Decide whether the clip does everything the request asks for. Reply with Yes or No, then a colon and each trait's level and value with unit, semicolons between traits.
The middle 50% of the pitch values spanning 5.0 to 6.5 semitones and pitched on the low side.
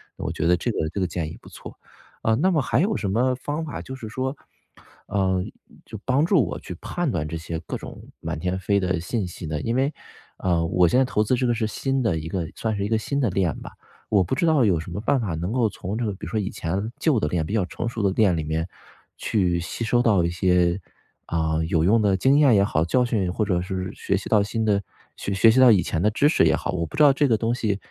Yes: average, 5.3 semitones; low, 100 Hz